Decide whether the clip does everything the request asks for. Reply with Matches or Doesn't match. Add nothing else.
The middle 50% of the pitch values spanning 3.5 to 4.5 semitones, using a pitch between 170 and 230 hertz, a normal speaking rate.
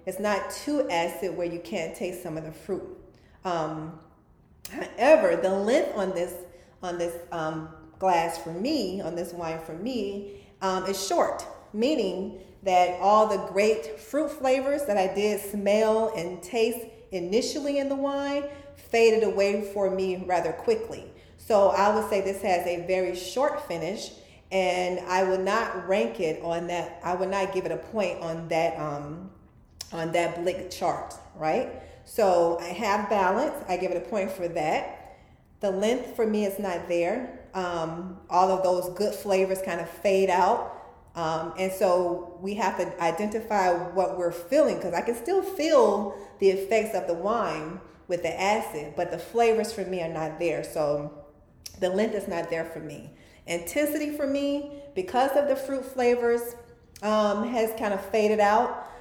Matches